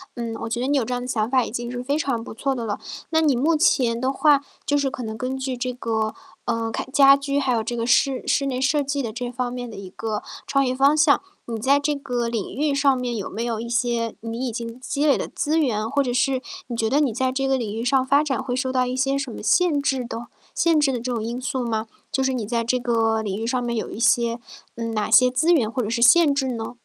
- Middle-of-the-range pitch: No, very high, 250 Hz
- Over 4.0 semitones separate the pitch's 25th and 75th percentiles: No, average, 3.0 semitones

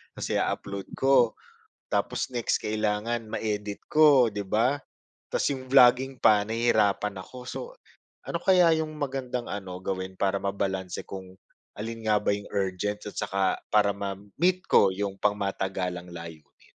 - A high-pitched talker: No, low, 105 Hz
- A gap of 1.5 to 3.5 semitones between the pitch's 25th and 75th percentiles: No, average, 4.2 semitones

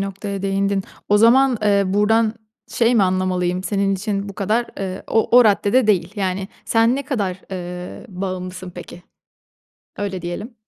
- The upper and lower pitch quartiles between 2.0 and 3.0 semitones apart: Yes, narrow, 2.5 semitones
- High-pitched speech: Yes, high, 195 Hz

